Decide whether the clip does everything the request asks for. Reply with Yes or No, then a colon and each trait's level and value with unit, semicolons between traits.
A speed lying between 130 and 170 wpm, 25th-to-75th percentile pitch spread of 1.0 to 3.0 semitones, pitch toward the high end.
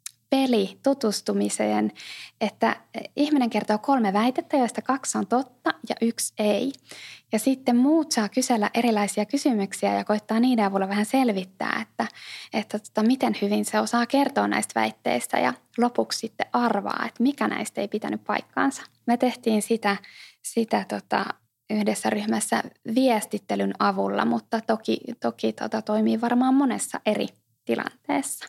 No: average, 135 wpm; average, 4.2 semitones; high, 220 Hz